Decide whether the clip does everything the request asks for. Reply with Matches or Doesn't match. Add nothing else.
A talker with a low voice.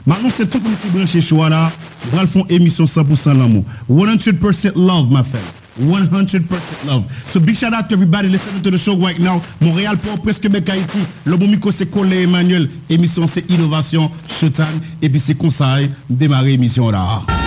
Doesn't match